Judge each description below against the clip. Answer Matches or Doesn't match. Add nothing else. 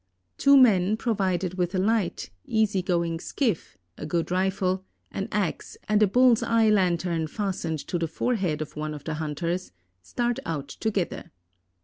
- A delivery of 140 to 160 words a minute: Matches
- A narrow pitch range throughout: Doesn't match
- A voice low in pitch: Doesn't match